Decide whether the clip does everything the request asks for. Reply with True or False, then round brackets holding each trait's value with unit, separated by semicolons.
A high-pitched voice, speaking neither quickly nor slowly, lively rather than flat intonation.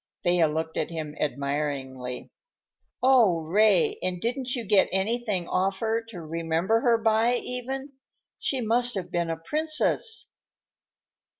False (195 Hz; 130 wpm; 6.7 semitones)